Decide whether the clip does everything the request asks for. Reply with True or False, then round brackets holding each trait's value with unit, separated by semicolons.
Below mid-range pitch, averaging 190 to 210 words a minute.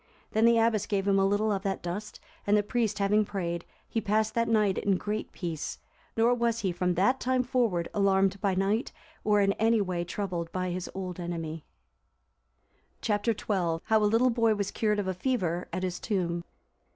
False (200 Hz; 195 wpm)